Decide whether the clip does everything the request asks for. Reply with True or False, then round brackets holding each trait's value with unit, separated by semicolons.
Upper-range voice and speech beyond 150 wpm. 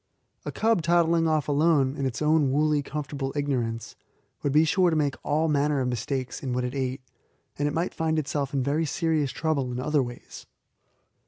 False (145 Hz; 190 wpm)